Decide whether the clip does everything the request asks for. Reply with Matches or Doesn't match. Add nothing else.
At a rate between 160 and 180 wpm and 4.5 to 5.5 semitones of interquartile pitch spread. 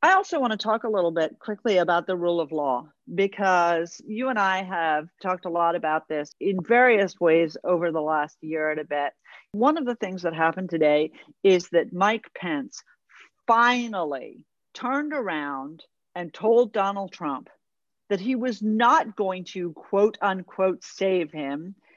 Matches